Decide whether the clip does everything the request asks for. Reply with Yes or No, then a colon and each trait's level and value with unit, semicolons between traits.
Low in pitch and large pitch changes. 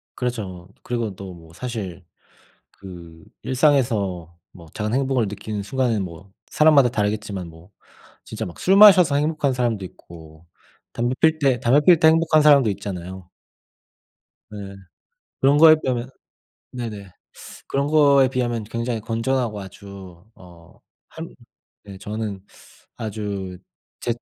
Yes: low, 110 Hz; wide, 5.7 semitones